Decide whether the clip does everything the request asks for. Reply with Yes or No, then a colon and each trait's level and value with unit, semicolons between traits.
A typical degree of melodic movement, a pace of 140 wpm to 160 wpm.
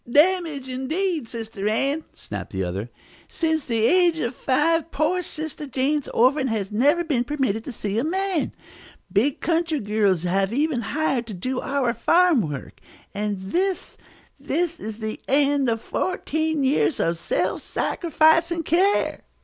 No: wide, 6.4 semitones; average, 150 wpm